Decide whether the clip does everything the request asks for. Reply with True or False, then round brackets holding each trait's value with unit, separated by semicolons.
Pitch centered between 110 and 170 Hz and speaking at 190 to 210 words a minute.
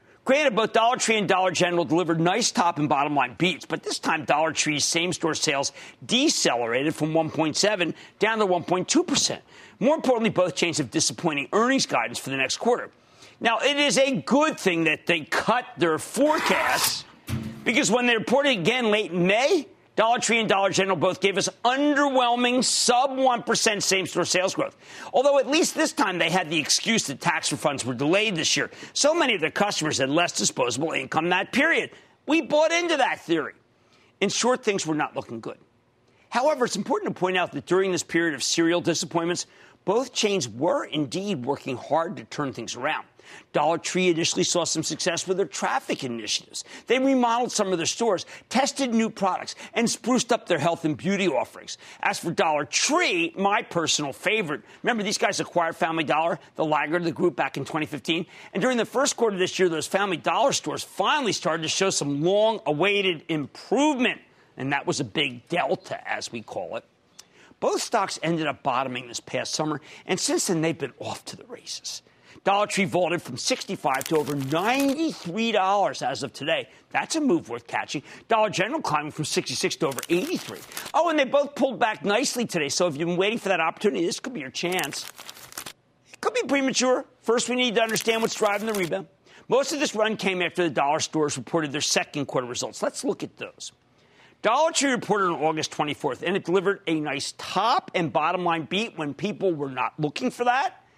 False (185 Hz; 195 wpm)